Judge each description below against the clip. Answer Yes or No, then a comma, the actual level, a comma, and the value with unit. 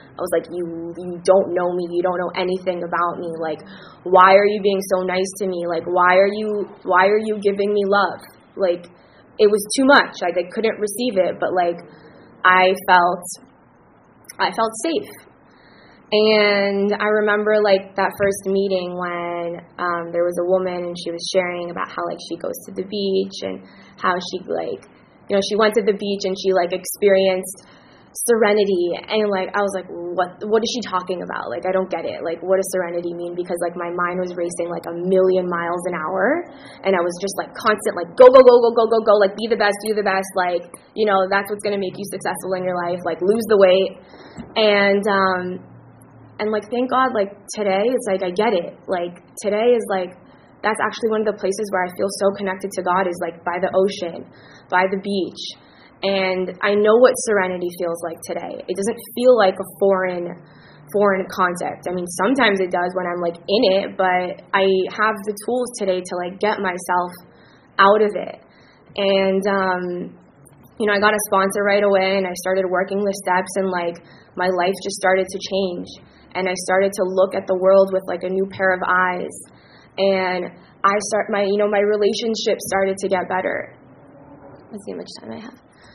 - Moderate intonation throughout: No, narrow, 2.2 semitones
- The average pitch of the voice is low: No, high, 190 Hz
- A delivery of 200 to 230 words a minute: Yes, fast, 205 wpm